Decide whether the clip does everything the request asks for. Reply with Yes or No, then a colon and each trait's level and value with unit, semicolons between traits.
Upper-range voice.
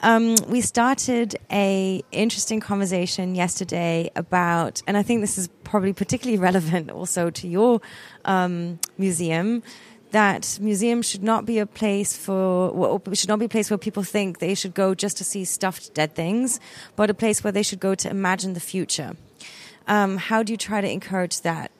Yes: high, 195 Hz